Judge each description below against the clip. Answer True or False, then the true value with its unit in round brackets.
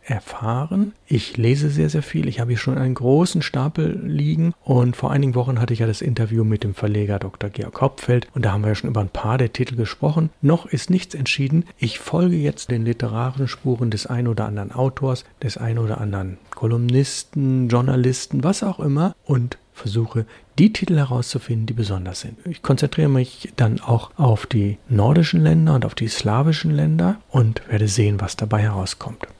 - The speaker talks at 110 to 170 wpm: False (190 wpm)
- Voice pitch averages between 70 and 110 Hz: False (125 Hz)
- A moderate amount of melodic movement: True (4.7 semitones)